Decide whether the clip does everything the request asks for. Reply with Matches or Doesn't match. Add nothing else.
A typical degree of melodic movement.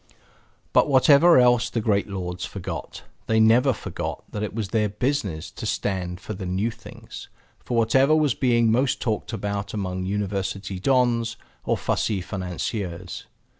Matches